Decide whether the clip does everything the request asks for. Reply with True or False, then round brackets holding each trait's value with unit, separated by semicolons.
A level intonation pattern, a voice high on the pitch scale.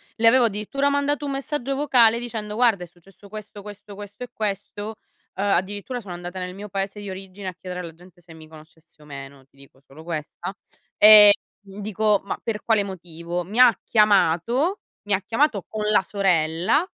False (3.9 semitones; 200 Hz)